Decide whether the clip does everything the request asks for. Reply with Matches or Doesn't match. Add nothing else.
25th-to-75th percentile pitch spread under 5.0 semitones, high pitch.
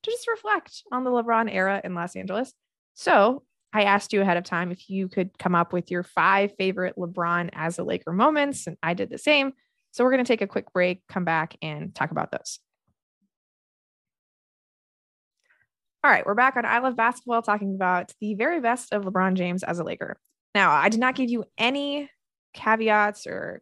Doesn't match